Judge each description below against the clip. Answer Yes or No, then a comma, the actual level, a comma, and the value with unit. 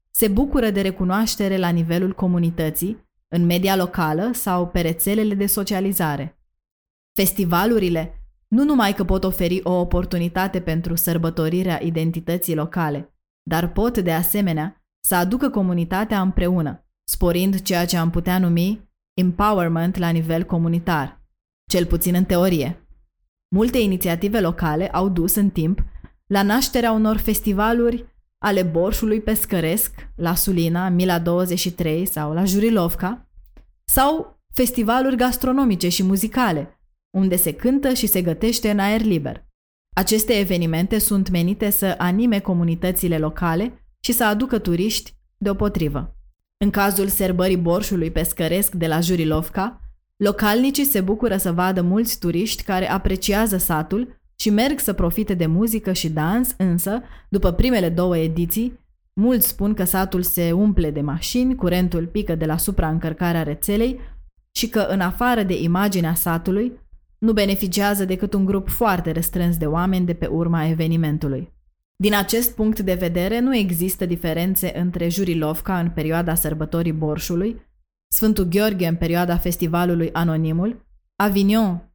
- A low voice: No, medium, 185 Hz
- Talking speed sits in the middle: Yes, average, 135 wpm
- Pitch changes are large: No, average, 3.5 semitones